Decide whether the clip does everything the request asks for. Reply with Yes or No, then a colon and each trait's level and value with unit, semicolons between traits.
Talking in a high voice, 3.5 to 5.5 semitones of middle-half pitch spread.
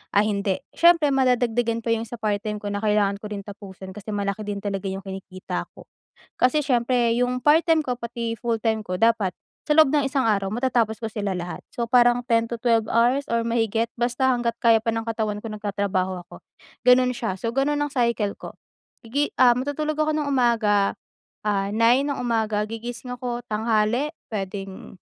No: high, 230 Hz; average, 3.1 semitones